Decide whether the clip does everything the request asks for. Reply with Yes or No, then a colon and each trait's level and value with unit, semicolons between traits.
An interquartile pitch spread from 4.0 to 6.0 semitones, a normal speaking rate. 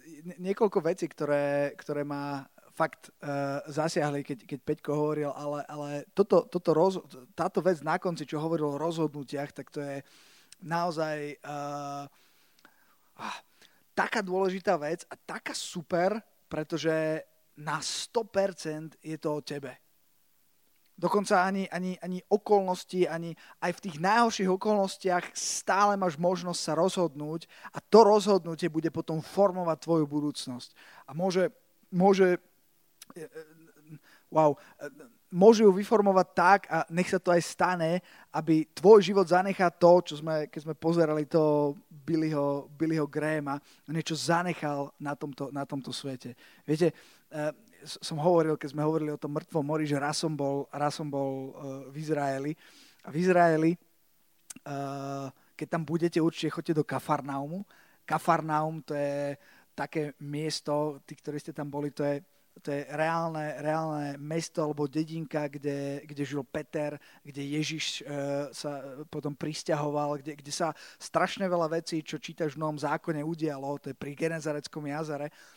No: average, 3.0 semitones; average, 140 wpm